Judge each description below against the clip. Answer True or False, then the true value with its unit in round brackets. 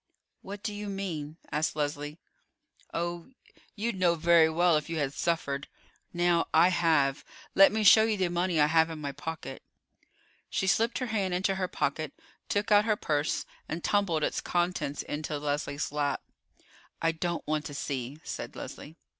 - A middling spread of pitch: True (4.3 semitones)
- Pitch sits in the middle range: True (165 Hz)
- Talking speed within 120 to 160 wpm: False (170 wpm)